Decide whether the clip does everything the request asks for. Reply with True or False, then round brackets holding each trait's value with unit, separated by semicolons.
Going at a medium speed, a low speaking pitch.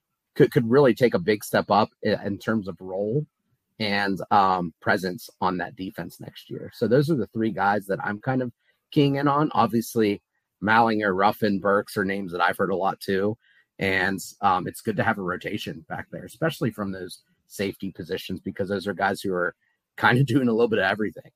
False (210 wpm; 100 Hz)